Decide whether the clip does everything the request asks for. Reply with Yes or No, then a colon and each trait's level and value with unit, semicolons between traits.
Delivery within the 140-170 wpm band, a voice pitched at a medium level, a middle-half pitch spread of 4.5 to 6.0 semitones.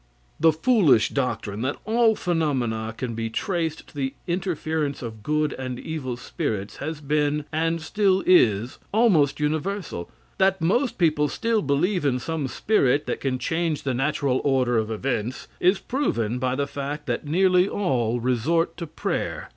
Yes: average, 155 wpm; medium, 150 Hz; average, 5.3 semitones